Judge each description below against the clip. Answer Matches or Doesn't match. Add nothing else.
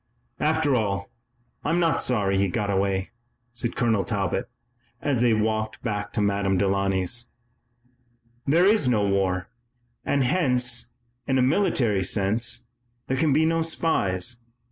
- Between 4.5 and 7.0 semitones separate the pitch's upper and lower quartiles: Matches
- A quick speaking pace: Doesn't match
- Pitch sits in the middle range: Doesn't match